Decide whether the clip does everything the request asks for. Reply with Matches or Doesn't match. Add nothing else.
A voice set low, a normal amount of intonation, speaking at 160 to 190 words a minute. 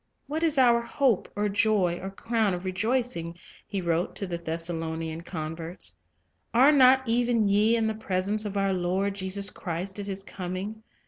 Doesn't match